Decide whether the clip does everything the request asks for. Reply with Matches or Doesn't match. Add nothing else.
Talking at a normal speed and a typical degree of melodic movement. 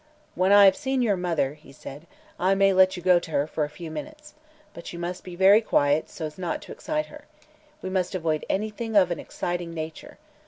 Doesn't match